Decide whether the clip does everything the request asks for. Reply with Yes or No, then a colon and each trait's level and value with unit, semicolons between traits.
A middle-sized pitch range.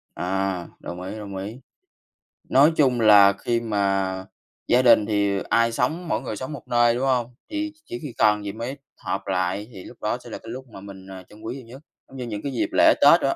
Yes: average, 4.3 semitones